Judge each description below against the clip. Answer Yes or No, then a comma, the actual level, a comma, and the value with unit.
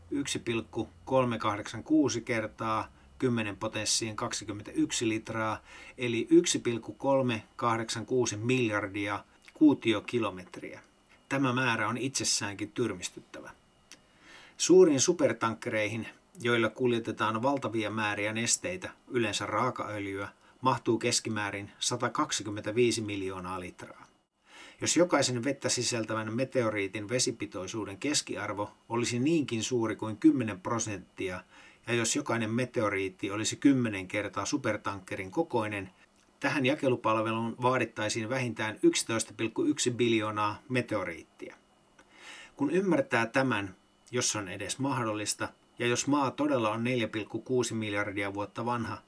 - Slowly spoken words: Yes, slow, 90 wpm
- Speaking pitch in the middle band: No, low, 115 Hz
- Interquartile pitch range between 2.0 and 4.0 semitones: Yes, average, 3.0 semitones